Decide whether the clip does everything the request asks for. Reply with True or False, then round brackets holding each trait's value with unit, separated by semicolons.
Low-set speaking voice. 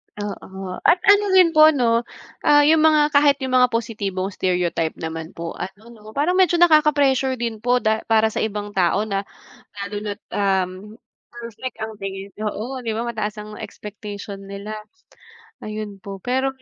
False (220 Hz)